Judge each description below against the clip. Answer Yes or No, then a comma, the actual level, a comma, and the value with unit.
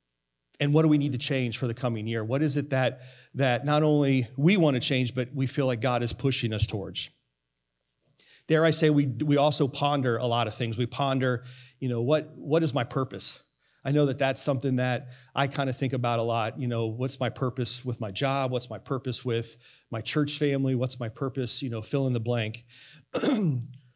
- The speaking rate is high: Yes, fast, 220 wpm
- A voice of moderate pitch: No, low, 130 Hz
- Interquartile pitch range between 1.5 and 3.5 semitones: Yes, average, 2.8 semitones